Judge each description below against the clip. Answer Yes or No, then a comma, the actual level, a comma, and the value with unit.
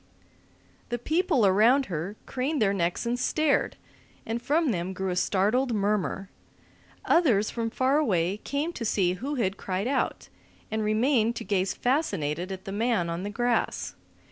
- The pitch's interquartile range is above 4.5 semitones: Yes, average, 5.2 semitones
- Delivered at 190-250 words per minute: No, average, 160 wpm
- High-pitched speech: Yes, high, 220 Hz